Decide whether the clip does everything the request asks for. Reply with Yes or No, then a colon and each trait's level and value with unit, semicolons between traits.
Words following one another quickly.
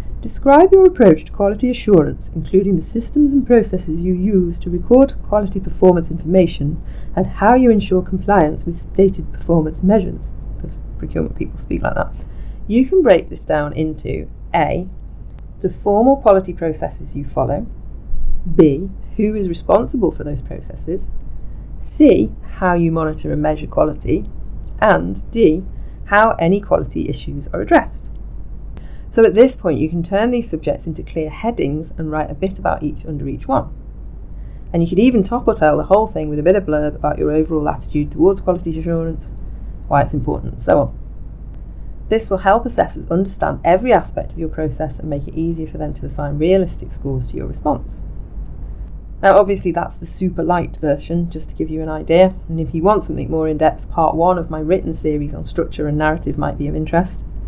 No: average, 185 wpm